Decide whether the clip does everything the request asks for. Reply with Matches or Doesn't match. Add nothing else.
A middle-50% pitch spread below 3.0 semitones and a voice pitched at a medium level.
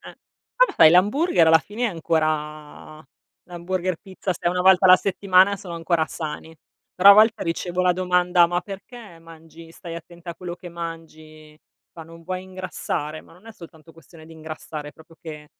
Matches